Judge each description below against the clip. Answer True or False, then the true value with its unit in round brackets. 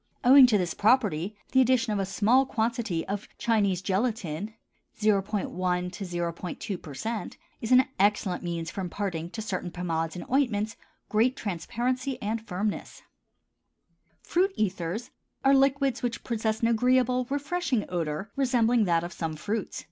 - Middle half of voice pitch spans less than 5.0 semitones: False (5.4 semitones)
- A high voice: True (215 Hz)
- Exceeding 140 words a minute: False (135 wpm)